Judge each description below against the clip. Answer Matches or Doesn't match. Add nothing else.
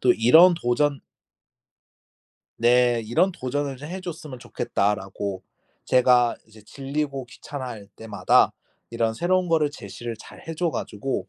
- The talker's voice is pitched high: Doesn't match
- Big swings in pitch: Doesn't match